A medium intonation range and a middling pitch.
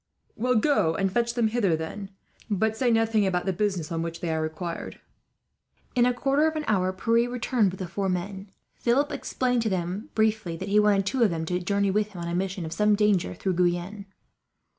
No: average, 4.2 semitones; high, 200 Hz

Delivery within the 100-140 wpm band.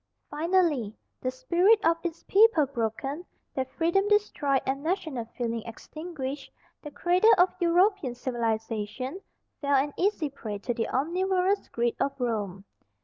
Yes: slow, 135 wpm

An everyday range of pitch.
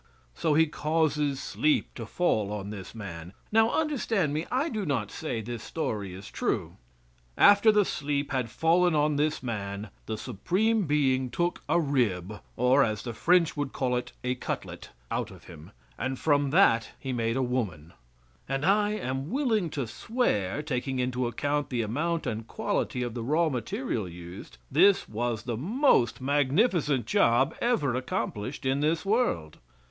No: wide, 6.1 semitones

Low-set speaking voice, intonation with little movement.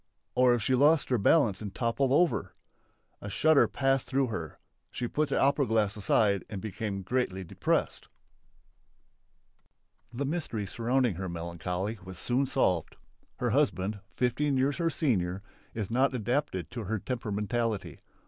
No: low, 115 Hz; average, 5.3 semitones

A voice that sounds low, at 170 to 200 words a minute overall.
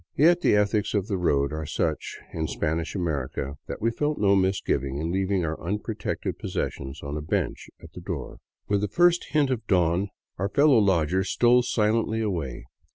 Yes: very low, 95 Hz; average, 180 wpm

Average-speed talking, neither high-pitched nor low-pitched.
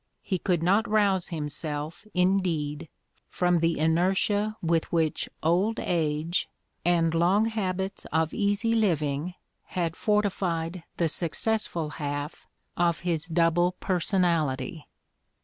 No: slow, 110 wpm; medium, 175 Hz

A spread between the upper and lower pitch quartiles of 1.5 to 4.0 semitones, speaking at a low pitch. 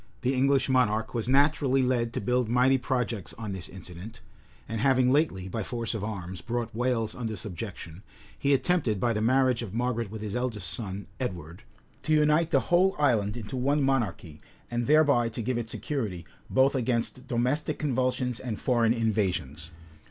Yes: average, 3.6 semitones; low, 120 Hz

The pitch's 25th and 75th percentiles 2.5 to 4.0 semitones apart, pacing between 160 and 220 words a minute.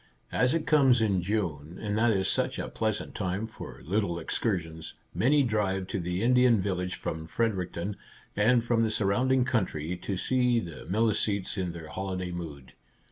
No: average, 4.5 semitones; average, 170 wpm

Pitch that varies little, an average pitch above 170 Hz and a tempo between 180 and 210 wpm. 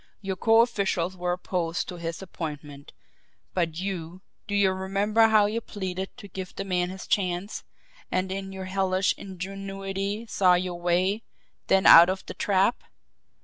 No: narrow, 1.7 semitones; high, 190 Hz; average, 155 wpm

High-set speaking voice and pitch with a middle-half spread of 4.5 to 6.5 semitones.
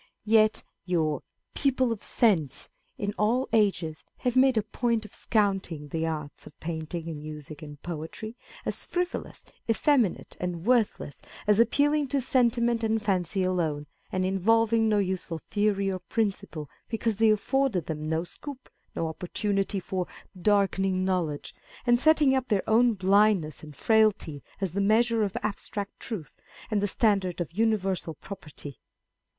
Yes: high, 200 Hz; average, 4.8 semitones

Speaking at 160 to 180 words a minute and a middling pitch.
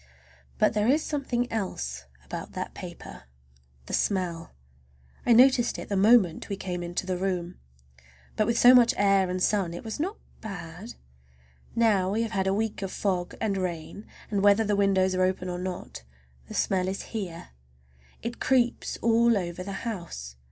No: average, 170 wpm; high, 195 Hz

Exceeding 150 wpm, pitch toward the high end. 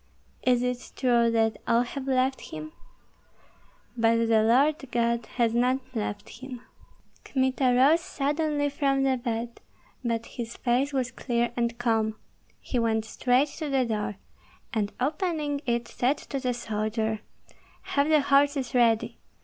No: average, 140 wpm; high, 245 Hz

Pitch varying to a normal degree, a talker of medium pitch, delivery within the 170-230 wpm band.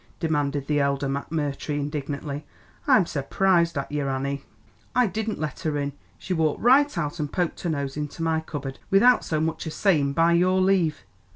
Yes: average, 3.8 semitones; medium, 155 Hz; average, 180 wpm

